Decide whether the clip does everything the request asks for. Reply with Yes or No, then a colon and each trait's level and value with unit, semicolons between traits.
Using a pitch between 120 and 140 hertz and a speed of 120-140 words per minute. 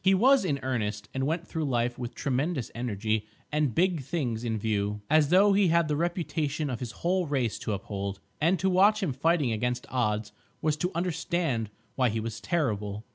No: low, 135 Hz; average, 190 wpm